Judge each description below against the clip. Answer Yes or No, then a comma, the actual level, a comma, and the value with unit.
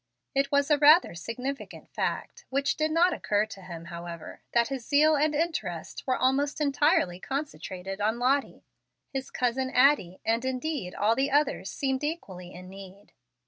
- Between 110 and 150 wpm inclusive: No, average, 160 wpm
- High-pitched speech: Yes, very high, 260 Hz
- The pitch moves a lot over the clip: Yes, wide, 6.8 semitones